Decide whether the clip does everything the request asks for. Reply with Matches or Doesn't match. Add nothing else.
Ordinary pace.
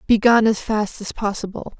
Matches